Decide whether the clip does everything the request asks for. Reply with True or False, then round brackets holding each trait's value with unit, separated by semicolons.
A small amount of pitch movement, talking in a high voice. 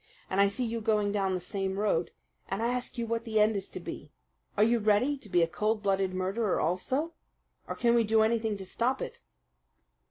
False (3.1 semitones; 215 Hz)